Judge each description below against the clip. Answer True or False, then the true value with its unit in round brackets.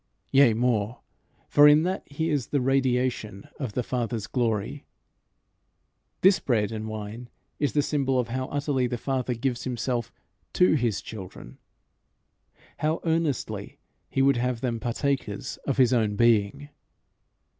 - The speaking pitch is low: True (125 Hz)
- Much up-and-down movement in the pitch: False (3.5 semitones)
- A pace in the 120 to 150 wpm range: True (140 wpm)